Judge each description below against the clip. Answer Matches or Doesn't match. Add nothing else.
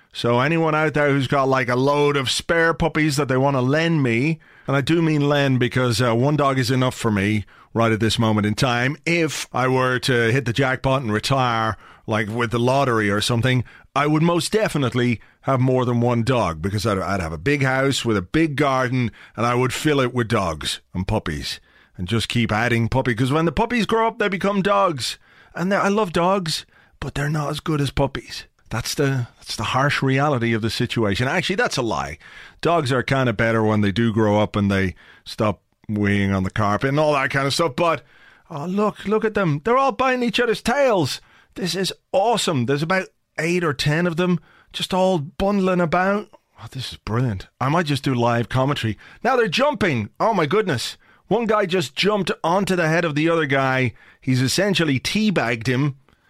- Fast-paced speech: Matches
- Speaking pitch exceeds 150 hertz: Doesn't match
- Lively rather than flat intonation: Matches